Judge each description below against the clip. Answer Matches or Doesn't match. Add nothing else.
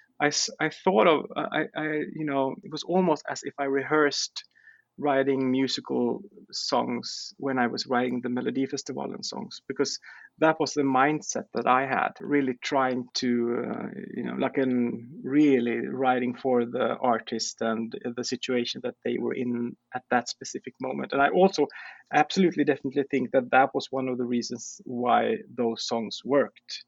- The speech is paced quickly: Matches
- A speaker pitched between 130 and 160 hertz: Matches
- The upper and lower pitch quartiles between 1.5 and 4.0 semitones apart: Matches